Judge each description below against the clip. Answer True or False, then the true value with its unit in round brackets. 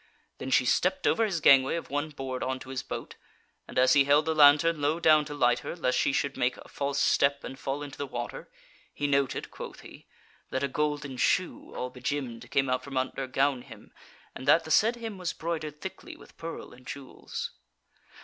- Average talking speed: False (210 wpm)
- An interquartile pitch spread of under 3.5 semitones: True (2.8 semitones)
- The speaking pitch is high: False (140 Hz)